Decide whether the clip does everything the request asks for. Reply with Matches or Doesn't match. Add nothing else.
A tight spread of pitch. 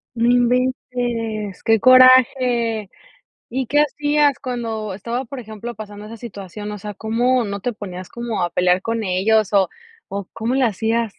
Doesn't match